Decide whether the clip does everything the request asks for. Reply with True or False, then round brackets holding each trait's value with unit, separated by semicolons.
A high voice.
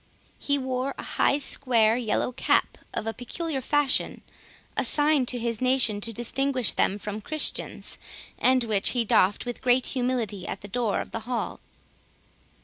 True (245 Hz)